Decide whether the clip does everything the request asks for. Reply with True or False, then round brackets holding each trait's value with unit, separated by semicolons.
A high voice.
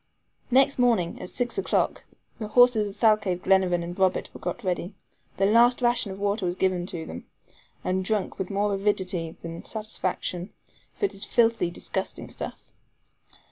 True (195 Hz)